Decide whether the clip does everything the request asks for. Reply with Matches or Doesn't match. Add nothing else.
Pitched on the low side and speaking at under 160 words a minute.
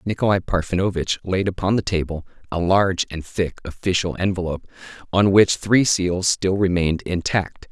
Matches